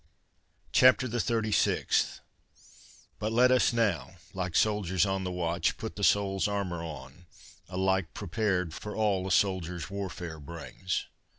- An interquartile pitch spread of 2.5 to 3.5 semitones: Yes, average, 3.2 semitones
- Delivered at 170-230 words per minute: No, slow, 135 wpm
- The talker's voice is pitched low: Yes, very low, 95 Hz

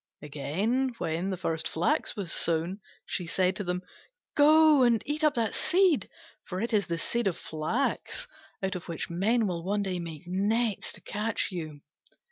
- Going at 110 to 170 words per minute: No, average, 180 wpm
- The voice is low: No, high, 190 Hz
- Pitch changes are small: No, wide, 5.6 semitones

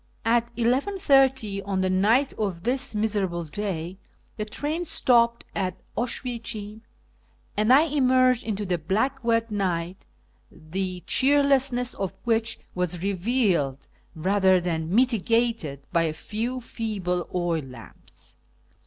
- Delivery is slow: Yes, slow, 120 wpm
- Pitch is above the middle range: Yes, high, 210 Hz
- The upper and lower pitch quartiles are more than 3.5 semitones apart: Yes, average, 5.2 semitones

